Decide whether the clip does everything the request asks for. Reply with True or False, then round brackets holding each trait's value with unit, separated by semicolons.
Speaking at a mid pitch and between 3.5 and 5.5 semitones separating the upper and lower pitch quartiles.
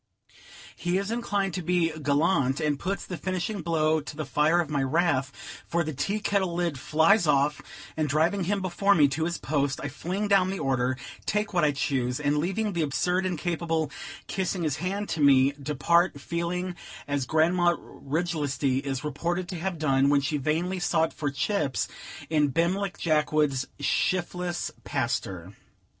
True (160 Hz; 4.0 semitones)